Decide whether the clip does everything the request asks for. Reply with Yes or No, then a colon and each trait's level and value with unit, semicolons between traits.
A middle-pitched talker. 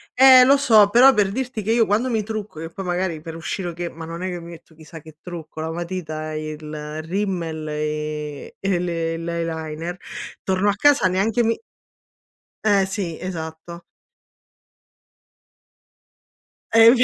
Yes: medium, 175 Hz